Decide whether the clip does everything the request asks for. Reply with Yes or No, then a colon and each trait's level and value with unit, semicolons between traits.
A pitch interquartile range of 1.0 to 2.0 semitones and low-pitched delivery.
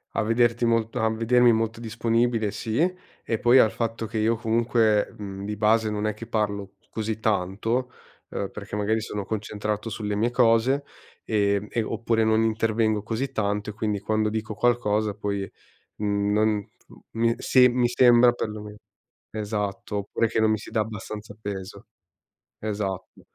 Yes: narrow, 1.7 semitones; low, 110 Hz